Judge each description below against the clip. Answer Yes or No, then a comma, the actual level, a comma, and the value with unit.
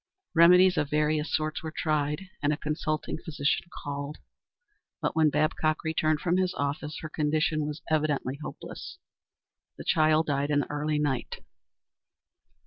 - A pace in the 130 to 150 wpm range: Yes, average, 140 wpm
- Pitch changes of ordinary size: No, narrow, 1.1 semitones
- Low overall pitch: No, medium, 155 Hz